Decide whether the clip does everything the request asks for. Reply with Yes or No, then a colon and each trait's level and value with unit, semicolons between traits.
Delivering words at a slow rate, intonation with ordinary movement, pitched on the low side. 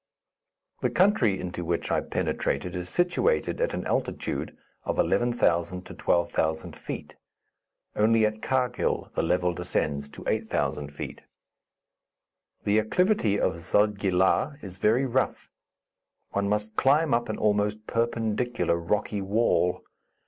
Yes: slow, 125 wpm; average, 5.0 semitones; low, 105 Hz